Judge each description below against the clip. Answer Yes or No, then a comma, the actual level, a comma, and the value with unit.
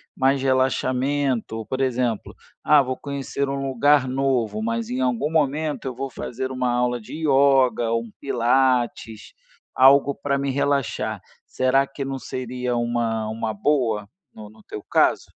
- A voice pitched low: Yes, low, 130 Hz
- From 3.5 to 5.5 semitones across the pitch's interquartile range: No, average, 2.7 semitones